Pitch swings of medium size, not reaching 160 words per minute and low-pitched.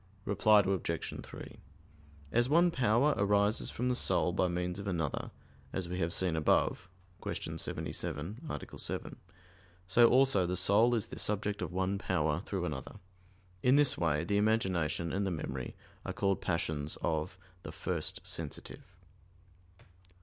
Yes: average, 4.0 semitones; average, 150 wpm; very low, 95 Hz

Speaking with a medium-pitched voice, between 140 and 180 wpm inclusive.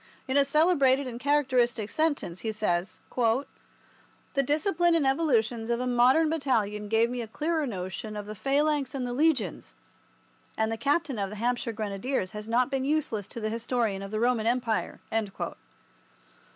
No: high, 245 Hz; average, 165 wpm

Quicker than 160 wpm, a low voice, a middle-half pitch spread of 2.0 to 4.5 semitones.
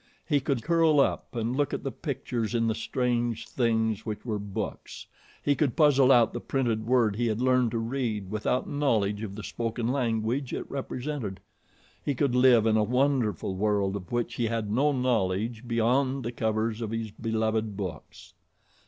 Yes: average, 180 wpm; low, 115 Hz; average, 3.0 semitones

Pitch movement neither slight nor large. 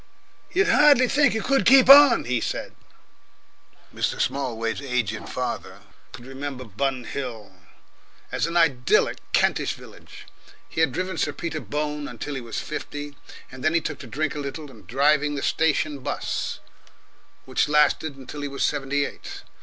Yes: average, 3.6 semitones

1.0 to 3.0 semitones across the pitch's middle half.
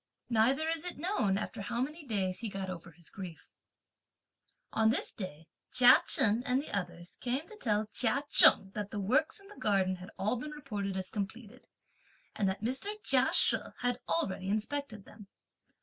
No: average, 5.1 semitones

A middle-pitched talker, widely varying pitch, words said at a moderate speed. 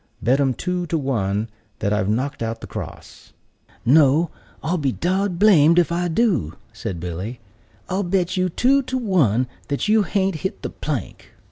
Yes: medium, 160 Hz; wide, 7.3 semitones; average, 175 wpm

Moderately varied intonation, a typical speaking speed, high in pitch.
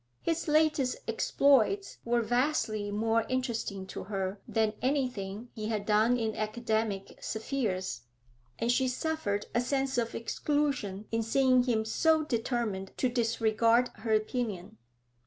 No: average, 3.2 semitones; slow, 130 wpm; high, 230 Hz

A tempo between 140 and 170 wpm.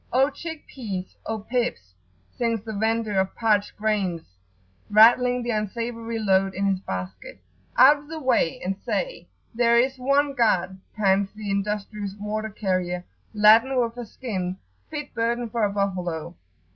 Yes: average, 150 wpm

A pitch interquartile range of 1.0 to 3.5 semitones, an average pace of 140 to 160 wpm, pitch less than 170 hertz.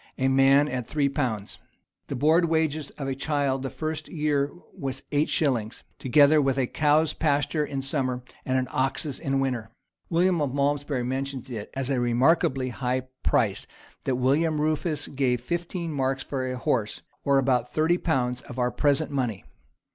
No: average, 2.7 semitones; average, 170 wpm; low, 135 Hz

